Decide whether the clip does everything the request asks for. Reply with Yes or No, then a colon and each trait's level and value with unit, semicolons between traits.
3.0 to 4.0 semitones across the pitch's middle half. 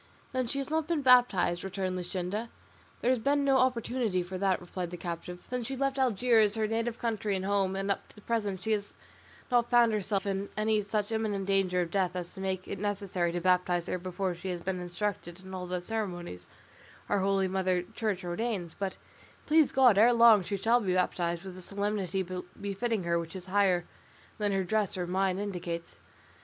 Yes: average, 3.6 semitones